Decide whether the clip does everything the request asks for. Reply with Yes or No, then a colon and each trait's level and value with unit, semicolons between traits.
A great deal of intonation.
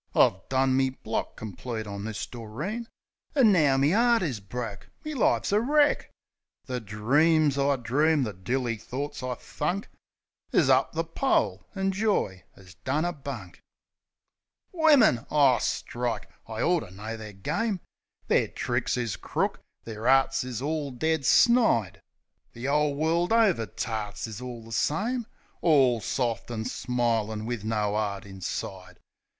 Yes: wide, 6.3 semitones